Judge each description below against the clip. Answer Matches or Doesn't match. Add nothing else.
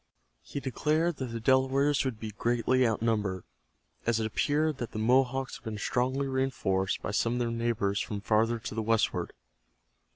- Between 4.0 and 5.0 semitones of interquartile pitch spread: Doesn't match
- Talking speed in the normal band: Matches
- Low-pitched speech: Matches